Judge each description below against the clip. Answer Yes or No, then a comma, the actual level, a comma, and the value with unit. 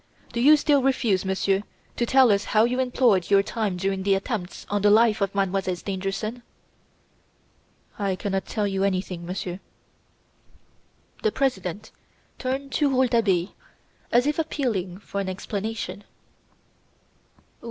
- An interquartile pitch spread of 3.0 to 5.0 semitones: Yes, average, 4.2 semitones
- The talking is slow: Yes, slow, 130 wpm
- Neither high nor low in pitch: No, high, 205 Hz